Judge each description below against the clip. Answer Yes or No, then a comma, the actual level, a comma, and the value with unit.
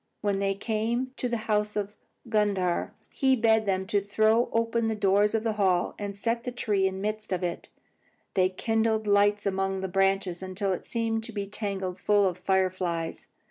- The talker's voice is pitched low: No, high, 205 Hz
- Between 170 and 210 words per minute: Yes, average, 190 wpm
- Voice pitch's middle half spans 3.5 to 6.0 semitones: No, narrow, 2.6 semitones